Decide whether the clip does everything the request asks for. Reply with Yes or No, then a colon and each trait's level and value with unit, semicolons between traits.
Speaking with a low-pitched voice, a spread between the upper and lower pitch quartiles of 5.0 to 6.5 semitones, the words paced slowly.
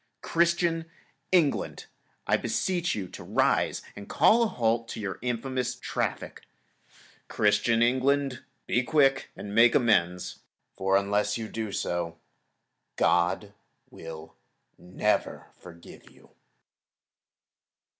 Yes: low, 115 Hz; average, 5.3 semitones; slow, 105 wpm